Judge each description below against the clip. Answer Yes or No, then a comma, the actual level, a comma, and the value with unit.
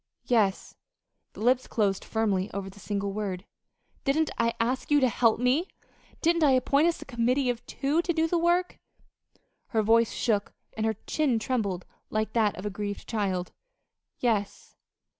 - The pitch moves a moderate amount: Yes, average, 4.9 semitones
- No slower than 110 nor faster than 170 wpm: Yes, average, 165 wpm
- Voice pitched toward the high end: Yes, high, 230 Hz